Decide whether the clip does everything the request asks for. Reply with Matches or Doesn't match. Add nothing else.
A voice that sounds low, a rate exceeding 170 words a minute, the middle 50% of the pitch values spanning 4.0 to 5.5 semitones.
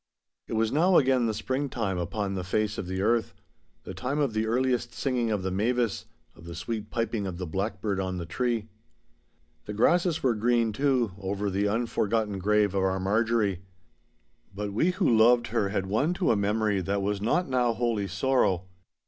Doesn't match